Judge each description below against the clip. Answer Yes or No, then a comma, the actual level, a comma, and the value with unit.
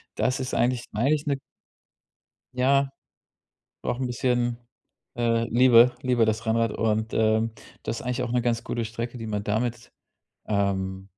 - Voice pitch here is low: Yes, low, 120 Hz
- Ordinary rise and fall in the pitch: No, narrow, 2.1 semitones